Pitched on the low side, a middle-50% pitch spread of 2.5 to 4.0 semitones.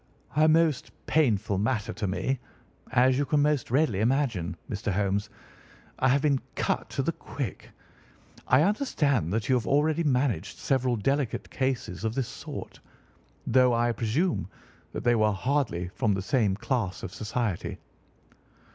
No: low, 125 Hz; average, 5.0 semitones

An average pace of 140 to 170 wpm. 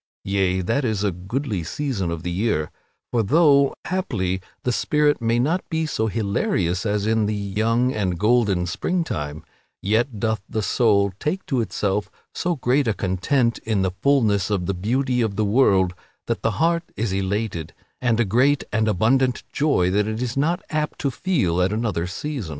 No: average, 180 wpm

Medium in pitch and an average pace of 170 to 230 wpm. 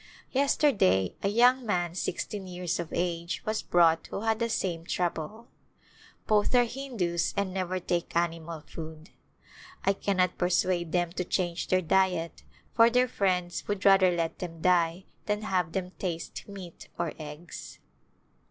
No: medium, 180 Hz; average, 150 wpm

